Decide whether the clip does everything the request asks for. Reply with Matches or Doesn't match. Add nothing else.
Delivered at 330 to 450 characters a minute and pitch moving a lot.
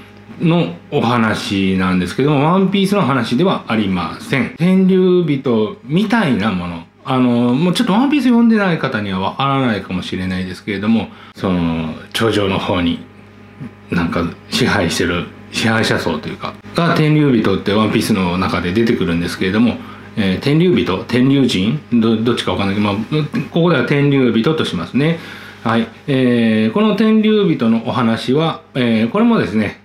Matches